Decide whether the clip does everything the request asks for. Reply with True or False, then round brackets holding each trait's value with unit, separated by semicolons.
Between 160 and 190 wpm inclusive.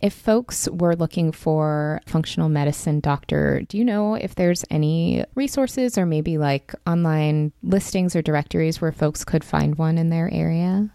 True (165 wpm)